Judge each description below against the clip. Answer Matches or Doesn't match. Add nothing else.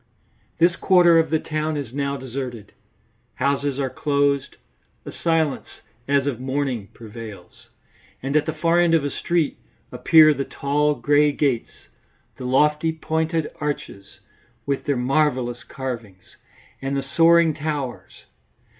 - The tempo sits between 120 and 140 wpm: Matches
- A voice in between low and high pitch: Matches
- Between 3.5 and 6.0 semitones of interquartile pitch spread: Doesn't match